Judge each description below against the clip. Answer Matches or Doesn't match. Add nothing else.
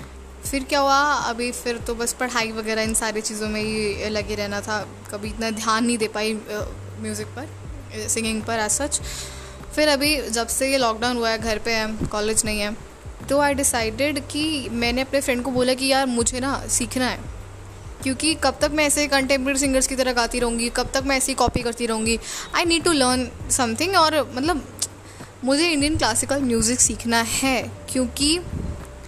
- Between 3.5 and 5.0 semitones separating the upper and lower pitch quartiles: Matches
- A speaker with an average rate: Matches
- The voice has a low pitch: Doesn't match